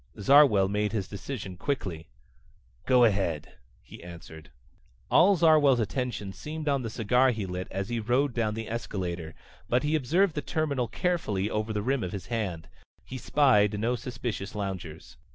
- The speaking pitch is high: No, low, 110 Hz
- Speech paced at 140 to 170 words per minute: Yes, average, 160 wpm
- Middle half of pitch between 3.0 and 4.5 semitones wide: No, wide, 5.6 semitones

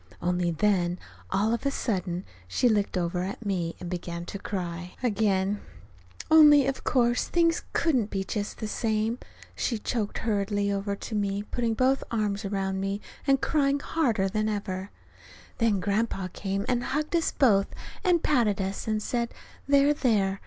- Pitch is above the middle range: Yes, high, 210 Hz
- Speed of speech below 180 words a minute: Yes, average, 165 wpm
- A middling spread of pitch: Yes, average, 4.0 semitones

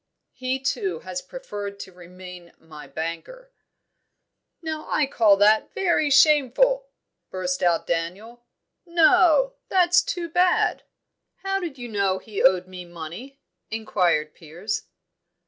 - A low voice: No, high, 220 Hz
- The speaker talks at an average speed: No, slow, 120 wpm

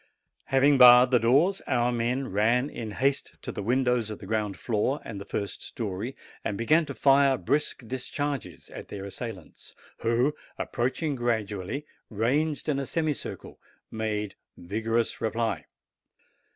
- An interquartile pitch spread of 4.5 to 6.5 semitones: No, average, 3.9 semitones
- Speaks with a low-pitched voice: Yes, low, 120 Hz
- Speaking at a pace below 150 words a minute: Yes, average, 140 wpm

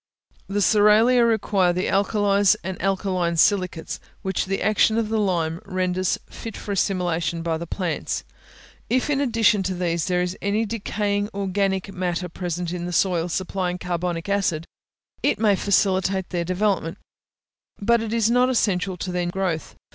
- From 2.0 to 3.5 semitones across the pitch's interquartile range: Yes, narrow, 2.5 semitones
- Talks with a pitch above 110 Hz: Yes, high, 190 Hz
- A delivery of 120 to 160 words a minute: Yes, average, 155 wpm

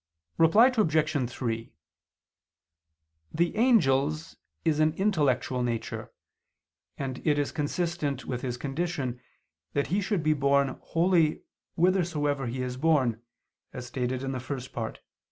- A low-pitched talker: No, medium, 145 Hz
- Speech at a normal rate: No, slow, 130 wpm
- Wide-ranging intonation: No, average, 4.3 semitones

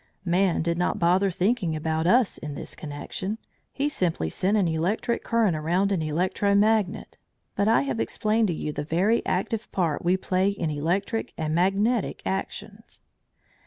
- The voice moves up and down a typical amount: Yes, average, 4.3 semitones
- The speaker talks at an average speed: Yes, average, 165 wpm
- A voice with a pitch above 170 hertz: Yes, medium, 185 Hz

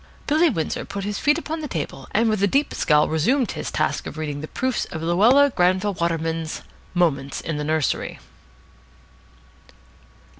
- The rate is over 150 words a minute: Yes, average, 160 wpm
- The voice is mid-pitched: Yes, medium, 180 Hz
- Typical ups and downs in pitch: No, wide, 7.8 semitones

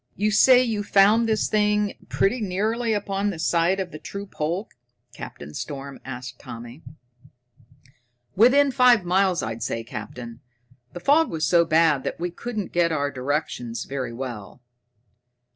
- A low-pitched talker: No, medium, 175 Hz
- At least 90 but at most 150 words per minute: Yes, average, 145 wpm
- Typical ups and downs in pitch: No, wide, 7.5 semitones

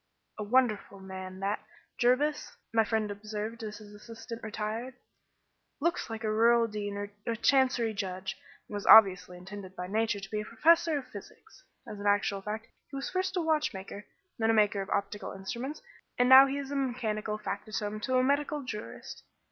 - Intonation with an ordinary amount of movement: Yes, average, 3.8 semitones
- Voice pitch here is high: Yes, high, 220 Hz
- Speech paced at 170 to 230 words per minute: Yes, average, 180 wpm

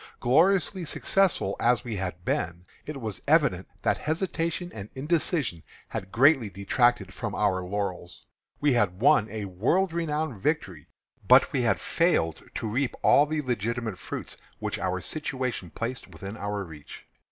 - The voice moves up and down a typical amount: No, wide, 7.6 semitones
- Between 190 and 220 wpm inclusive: No, average, 150 wpm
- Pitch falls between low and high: No, low, 115 Hz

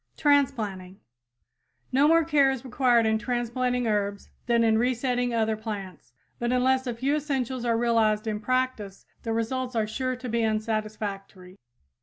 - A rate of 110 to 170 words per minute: Yes, average, 150 wpm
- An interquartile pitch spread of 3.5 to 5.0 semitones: No, average, 3.0 semitones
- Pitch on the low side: No, high, 235 Hz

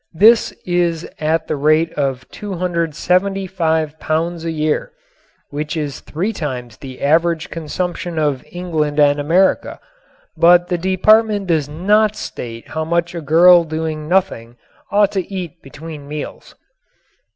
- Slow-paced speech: Yes, slow, 130 wpm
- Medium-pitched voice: Yes, medium, 165 Hz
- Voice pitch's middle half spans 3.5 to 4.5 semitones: No, average, 3.0 semitones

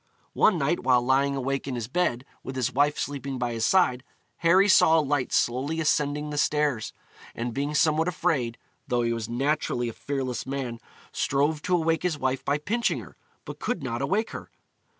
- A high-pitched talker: No, medium, 140 Hz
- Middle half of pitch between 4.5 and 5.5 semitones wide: No, average, 3.8 semitones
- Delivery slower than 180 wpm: No, average, 190 wpm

